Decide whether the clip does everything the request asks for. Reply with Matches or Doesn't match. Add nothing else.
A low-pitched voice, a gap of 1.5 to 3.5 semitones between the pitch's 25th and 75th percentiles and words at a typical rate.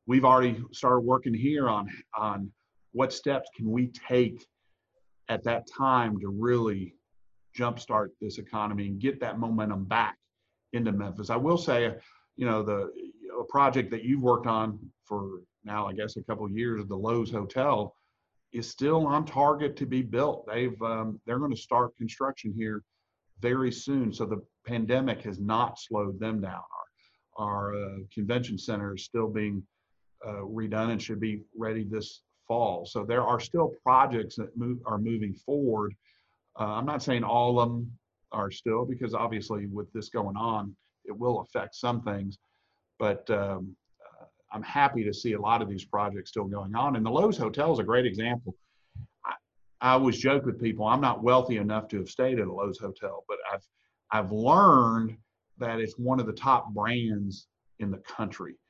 Matches